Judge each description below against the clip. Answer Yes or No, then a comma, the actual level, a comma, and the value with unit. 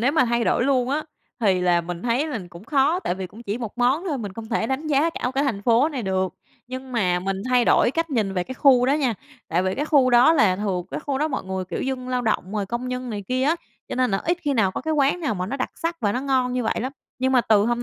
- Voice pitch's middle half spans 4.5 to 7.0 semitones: Yes, average, 5.0 semitones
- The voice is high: Yes, very high, 250 Hz